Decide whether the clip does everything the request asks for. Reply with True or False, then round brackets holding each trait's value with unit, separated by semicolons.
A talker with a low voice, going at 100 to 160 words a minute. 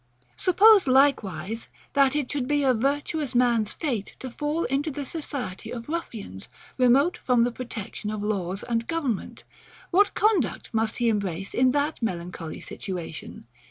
False (250 Hz; 150 wpm)